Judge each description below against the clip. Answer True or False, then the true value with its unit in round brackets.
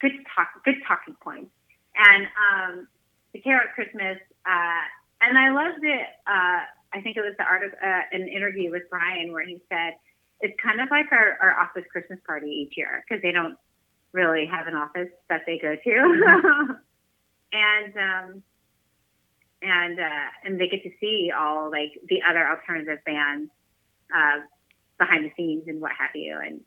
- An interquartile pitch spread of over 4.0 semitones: True (4.5 semitones)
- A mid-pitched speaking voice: True (180 Hz)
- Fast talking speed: False (175 wpm)